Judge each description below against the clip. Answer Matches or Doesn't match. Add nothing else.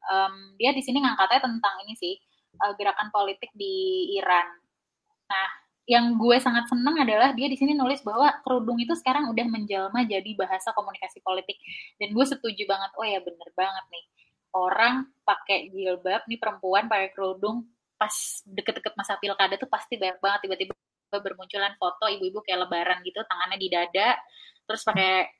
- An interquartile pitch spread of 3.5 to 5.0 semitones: Matches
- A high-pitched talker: Matches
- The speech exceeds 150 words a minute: Matches